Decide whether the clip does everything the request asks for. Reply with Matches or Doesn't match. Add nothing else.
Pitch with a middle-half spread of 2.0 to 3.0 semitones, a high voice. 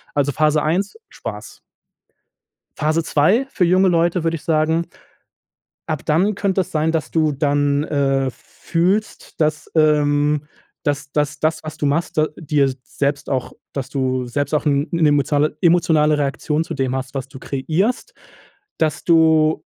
Doesn't match